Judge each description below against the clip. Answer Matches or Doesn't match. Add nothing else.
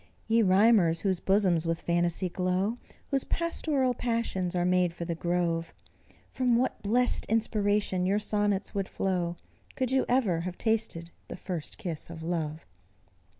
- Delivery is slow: Doesn't match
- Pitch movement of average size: Matches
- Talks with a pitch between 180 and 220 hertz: Matches